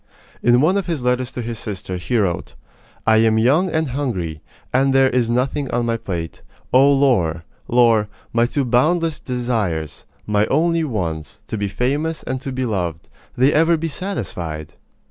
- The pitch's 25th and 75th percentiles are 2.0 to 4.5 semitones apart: No, average, 5.2 semitones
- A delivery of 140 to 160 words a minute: No, average, 170 wpm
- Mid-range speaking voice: No, low, 120 Hz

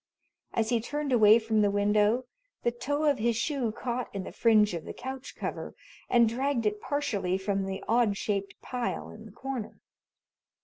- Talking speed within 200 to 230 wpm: No, average, 180 wpm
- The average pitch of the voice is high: Yes, high, 225 Hz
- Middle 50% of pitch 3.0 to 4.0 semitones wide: Yes, average, 3.3 semitones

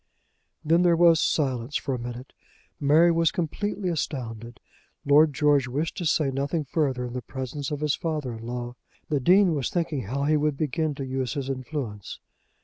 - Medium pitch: Yes, medium, 145 Hz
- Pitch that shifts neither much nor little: Yes, average, 3.8 semitones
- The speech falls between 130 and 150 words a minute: No, average, 180 wpm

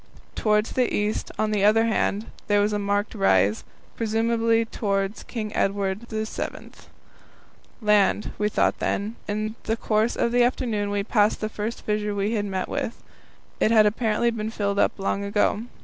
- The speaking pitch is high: Yes, high, 210 Hz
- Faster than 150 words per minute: Yes, average, 165 wpm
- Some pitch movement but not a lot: No, narrow, 1.7 semitones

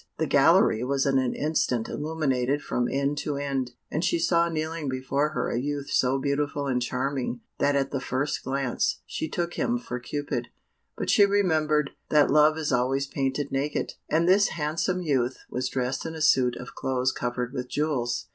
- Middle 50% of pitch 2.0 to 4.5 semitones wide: Yes, average, 3.1 semitones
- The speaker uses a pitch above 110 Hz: Yes, medium, 140 Hz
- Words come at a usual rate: Yes, average, 185 wpm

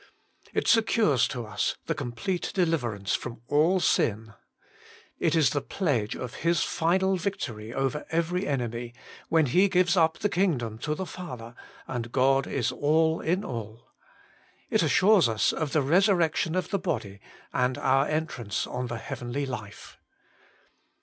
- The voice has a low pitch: No, medium, 145 Hz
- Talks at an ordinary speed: Yes, average, 150 wpm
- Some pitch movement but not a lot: No, wide, 6.4 semitones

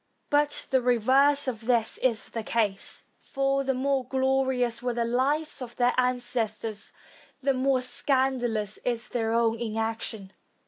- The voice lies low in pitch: No, high, 245 Hz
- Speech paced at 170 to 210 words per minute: No, average, 140 wpm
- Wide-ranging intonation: No, average, 2.8 semitones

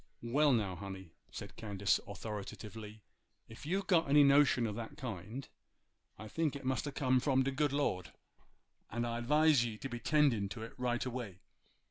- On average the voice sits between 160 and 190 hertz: No, low, 120 Hz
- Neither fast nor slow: Yes, average, 175 wpm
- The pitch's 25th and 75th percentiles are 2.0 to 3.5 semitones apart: No, average, 4.7 semitones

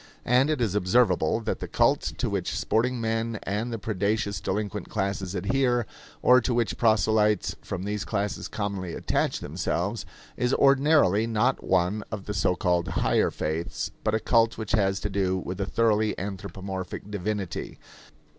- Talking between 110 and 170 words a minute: Yes, average, 160 wpm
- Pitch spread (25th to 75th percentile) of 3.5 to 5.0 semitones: No, average, 3.0 semitones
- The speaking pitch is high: No, low, 105 Hz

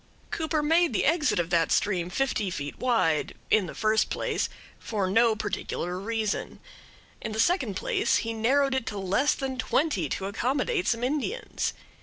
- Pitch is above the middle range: Yes, high, 225 Hz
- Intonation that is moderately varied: No, wide, 6.1 semitones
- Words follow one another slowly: No, average, 165 wpm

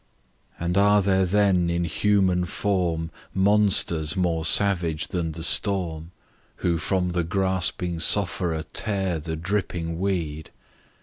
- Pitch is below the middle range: Yes, very low, 90 Hz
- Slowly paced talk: Yes, slow, 120 wpm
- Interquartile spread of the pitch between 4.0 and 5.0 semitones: No, average, 2.9 semitones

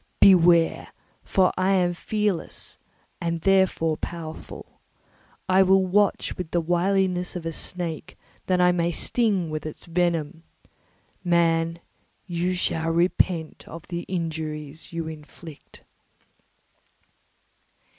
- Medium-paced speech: No, slow, 110 wpm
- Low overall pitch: No, medium, 170 Hz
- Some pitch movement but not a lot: No, narrow, 2.0 semitones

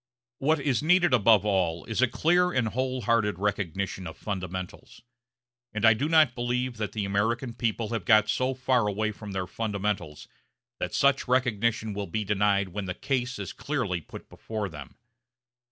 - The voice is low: Yes, low, 110 Hz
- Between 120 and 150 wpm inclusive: No, average, 170 wpm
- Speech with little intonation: No, average, 4.3 semitones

